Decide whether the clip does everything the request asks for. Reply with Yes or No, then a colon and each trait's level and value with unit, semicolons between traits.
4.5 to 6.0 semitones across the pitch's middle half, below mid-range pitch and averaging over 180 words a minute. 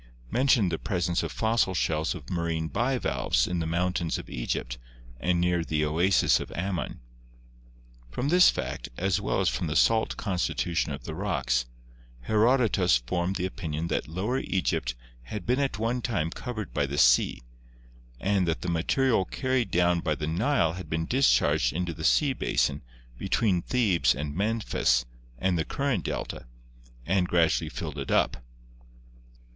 No: average, 5.2 semitones; very low, 90 Hz; average, 160 wpm